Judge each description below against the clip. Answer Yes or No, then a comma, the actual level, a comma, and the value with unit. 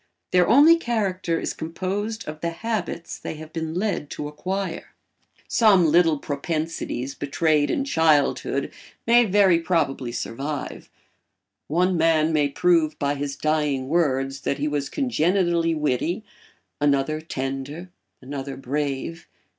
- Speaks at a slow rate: Yes, slow, 125 wpm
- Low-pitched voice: No, medium, 160 Hz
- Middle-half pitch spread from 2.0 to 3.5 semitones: No, average, 4.0 semitones